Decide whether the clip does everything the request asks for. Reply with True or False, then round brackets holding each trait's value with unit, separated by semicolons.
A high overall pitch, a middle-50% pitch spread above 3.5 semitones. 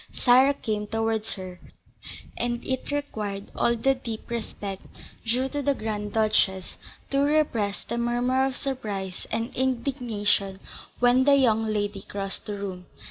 True (225 Hz; 4.0 semitones)